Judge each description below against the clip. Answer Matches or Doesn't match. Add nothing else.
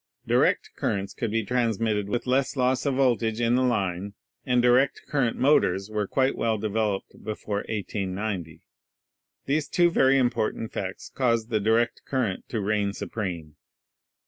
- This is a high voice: Doesn't match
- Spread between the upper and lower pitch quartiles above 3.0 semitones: Matches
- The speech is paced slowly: Doesn't match